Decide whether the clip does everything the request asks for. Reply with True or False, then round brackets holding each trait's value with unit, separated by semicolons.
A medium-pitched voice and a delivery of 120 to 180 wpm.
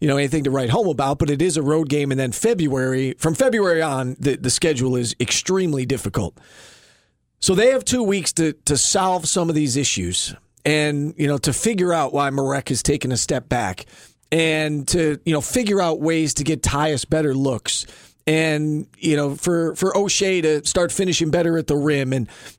False (150 Hz; 200 wpm)